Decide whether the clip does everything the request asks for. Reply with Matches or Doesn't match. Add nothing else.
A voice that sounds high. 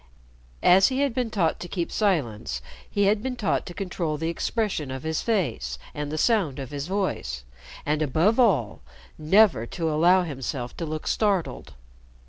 Doesn't match